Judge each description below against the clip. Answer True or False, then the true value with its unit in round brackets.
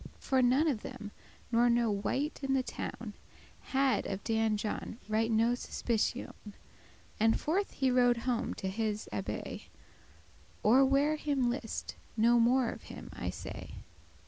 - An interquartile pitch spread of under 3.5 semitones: True (3.1 semitones)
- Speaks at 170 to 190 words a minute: False (150 wpm)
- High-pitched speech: True (240 Hz)